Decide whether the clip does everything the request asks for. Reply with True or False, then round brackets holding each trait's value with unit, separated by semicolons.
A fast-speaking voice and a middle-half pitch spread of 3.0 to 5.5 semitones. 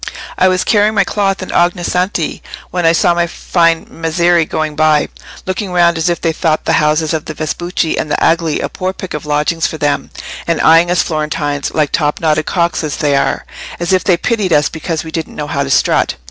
False (215 wpm; 2.4 semitones)